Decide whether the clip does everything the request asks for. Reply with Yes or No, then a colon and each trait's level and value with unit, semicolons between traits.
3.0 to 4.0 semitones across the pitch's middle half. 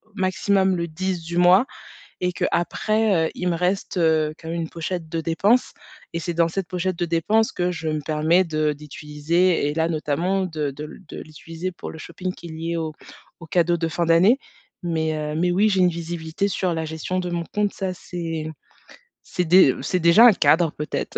No: narrow, 2.4 semitones